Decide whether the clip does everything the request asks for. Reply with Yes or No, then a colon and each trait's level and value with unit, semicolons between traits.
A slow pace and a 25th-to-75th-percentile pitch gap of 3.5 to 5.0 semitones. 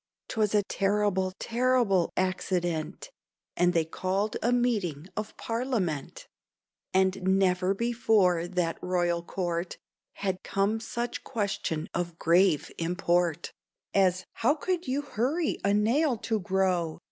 Yes: slow, 120 wpm; average, 4.2 semitones